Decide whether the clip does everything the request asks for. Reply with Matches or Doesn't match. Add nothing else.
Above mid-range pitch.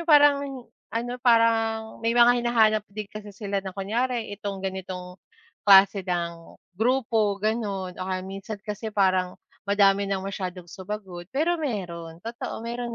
Matches